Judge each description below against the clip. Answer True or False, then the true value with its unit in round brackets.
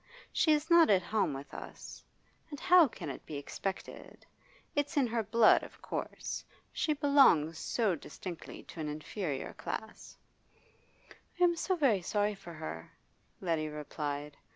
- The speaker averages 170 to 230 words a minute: False (150 wpm)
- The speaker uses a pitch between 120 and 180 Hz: False (200 Hz)